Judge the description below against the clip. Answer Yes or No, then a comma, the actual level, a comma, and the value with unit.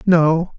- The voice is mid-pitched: Yes, medium, 170 Hz